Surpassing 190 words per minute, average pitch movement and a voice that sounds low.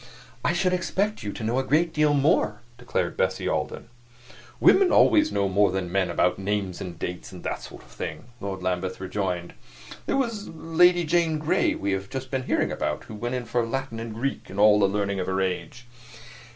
No: fast, 205 wpm; wide, 8.0 semitones; low, 110 Hz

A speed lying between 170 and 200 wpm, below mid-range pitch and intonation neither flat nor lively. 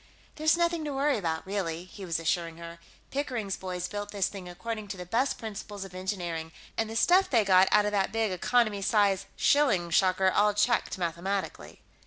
No: average, 190 wpm; high, 200 Hz; average, 3.8 semitones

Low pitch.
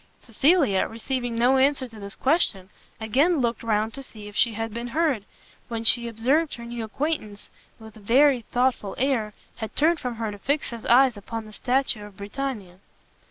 No: high, 235 Hz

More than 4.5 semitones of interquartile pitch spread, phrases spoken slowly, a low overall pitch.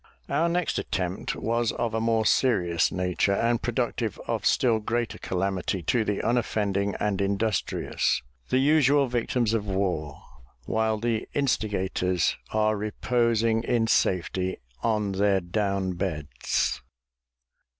No: average, 3.5 semitones; slow, 120 wpm; low, 110 Hz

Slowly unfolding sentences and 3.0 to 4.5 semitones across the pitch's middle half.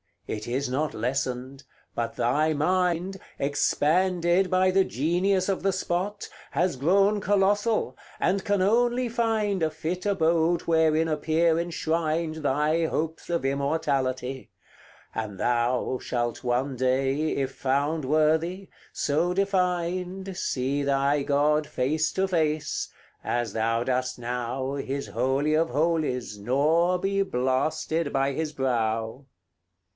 No: slow, 120 wpm; average, 5.2 semitones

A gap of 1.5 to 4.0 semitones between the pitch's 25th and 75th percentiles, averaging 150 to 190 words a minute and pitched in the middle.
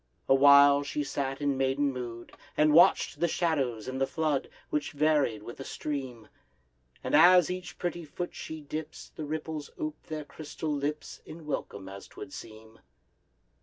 Yes: average, 2.8 semitones; average, 160 wpm; medium, 145 Hz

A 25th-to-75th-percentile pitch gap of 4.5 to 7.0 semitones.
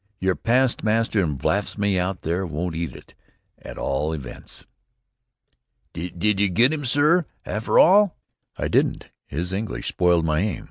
Yes: average, 5.1 semitones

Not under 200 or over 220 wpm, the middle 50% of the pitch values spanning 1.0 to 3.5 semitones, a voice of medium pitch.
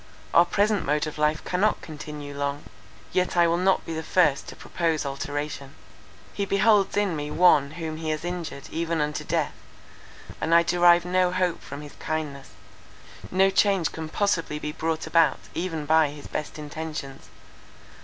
No: average, 165 wpm; average, 3.0 semitones; medium, 160 Hz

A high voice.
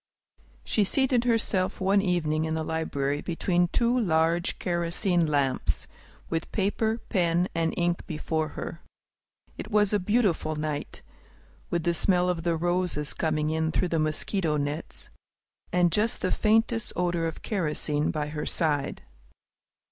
No: medium, 170 Hz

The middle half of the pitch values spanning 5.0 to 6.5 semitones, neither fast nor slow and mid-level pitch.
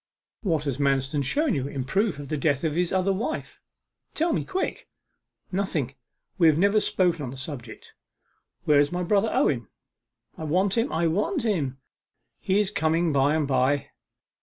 Yes: wide, 5.6 semitones; average, 175 wpm; medium, 160 Hz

